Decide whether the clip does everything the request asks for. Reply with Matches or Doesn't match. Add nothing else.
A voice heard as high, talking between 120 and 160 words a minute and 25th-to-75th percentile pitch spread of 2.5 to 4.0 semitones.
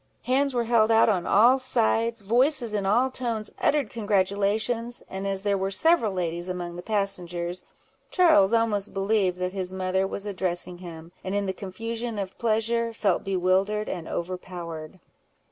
Matches